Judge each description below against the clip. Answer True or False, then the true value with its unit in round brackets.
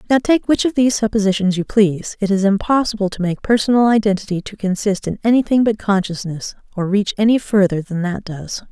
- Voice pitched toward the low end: False (205 Hz)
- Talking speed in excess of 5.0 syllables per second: True (5.9 syllables/s)